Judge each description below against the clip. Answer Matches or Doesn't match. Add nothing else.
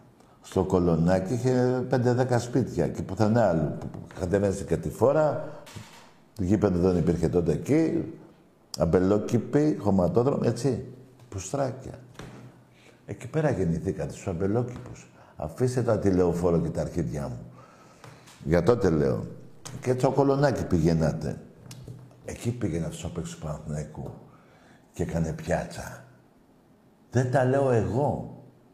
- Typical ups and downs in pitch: Doesn't match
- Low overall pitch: Matches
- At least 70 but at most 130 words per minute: Matches